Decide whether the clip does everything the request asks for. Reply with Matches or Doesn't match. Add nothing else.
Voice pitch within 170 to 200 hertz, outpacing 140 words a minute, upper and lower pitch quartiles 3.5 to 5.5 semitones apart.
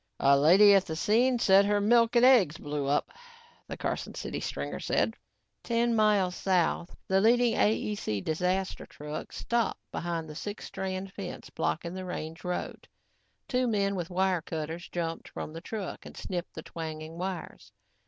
Matches